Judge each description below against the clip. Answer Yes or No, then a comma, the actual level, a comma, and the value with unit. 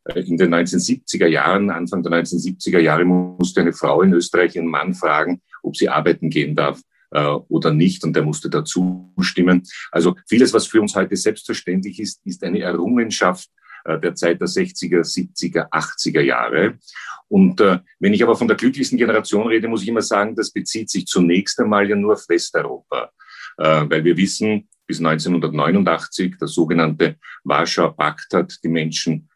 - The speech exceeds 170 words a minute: No, average, 165 wpm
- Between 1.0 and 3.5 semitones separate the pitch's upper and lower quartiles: No, average, 4.1 semitones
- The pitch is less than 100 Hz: Yes, very low, 90 Hz